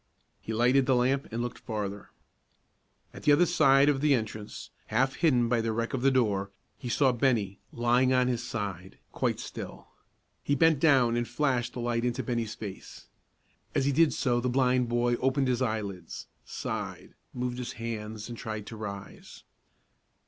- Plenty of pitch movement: No, average, 3.1 semitones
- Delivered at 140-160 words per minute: No, average, 175 wpm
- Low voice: Yes, low, 120 Hz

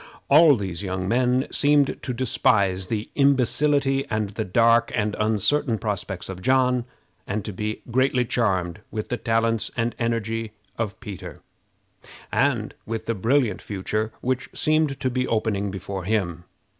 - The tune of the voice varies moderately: Yes, average, 4.1 semitones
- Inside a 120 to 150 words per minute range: Yes, average, 145 wpm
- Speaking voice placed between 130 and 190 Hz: No, low, 115 Hz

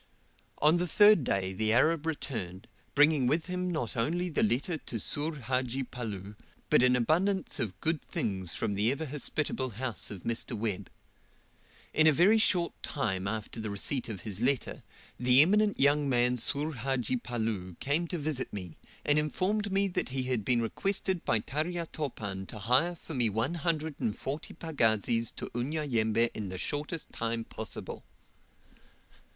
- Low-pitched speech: Yes, low, 130 Hz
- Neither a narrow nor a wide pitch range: No, wide, 6.0 semitones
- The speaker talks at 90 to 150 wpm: No, average, 165 wpm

